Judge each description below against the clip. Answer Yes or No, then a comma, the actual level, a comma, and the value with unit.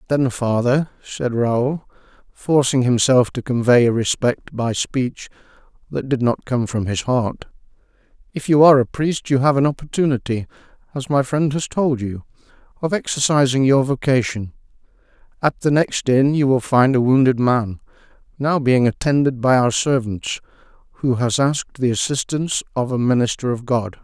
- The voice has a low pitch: Yes, low, 130 Hz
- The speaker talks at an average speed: Yes, average, 160 wpm